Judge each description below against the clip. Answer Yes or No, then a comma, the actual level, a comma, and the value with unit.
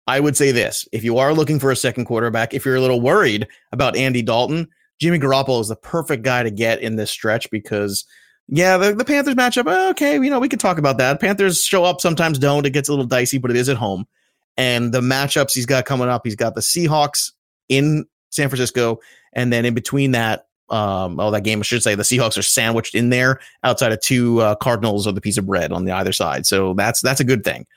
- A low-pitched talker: Yes, low, 130 Hz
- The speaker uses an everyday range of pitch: Yes, average, 4.3 semitones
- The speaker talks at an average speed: No, fast, 240 wpm